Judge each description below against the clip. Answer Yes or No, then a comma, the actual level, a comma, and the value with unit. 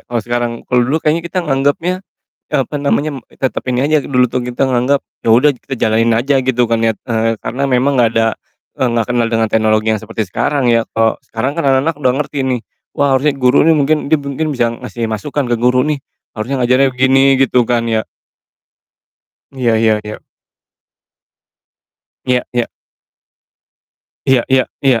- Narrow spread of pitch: No, average, 3.0 semitones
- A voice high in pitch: No, low, 125 Hz